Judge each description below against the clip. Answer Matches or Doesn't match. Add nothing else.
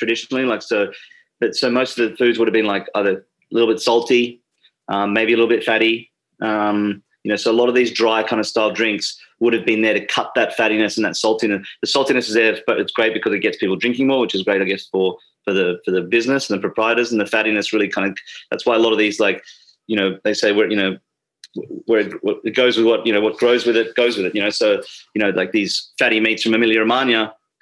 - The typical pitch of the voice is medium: Doesn't match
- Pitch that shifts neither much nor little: Doesn't match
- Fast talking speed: Matches